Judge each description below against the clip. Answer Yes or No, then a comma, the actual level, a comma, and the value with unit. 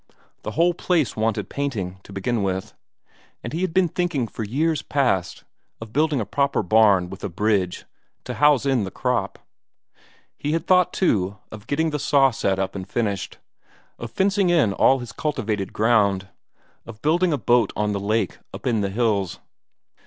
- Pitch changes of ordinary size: No, wide, 6.9 semitones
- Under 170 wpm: No, average, 175 wpm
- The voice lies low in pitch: Yes, low, 115 Hz